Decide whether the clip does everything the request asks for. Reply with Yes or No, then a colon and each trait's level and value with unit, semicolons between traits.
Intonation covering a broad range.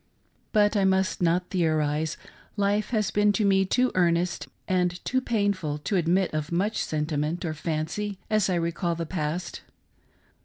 No: average, 3.7 semitones